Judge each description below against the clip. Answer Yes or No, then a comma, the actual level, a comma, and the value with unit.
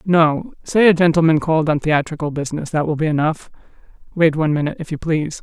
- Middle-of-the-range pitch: Yes, medium, 155 Hz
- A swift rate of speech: No, average, 190 wpm